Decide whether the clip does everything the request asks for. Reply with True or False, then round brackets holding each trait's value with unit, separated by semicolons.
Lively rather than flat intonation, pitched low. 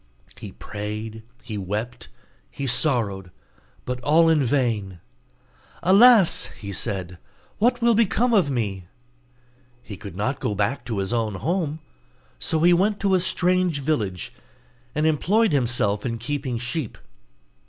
True (8.4 semitones; 125 Hz)